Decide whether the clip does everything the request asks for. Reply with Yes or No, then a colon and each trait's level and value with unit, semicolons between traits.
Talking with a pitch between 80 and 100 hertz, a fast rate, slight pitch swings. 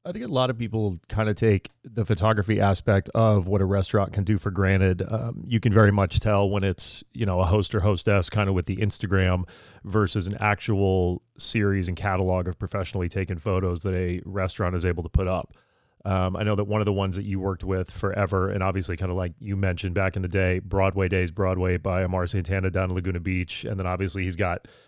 Yes: very low, 95 Hz; fast, 230 wpm; narrow, 1.9 semitones